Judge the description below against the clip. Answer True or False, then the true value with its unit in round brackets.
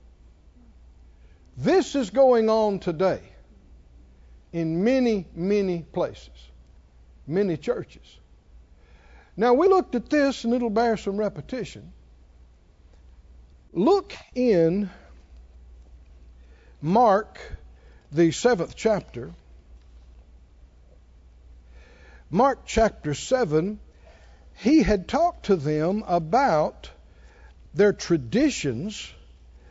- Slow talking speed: True (75 wpm)